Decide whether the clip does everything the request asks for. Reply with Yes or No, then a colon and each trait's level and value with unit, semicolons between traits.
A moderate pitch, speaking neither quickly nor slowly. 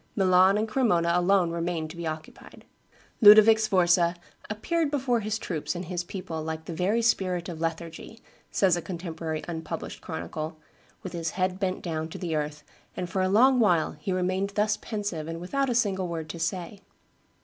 Yes: medium, 180 Hz; average, 180 wpm